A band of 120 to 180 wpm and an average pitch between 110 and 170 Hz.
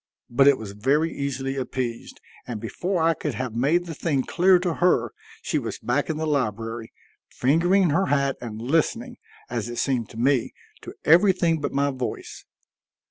Yes: average, 175 wpm; medium, 140 Hz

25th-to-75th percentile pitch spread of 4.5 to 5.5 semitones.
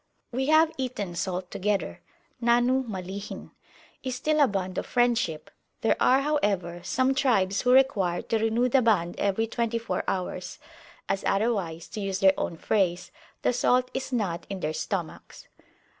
Yes: average, 5.1 semitones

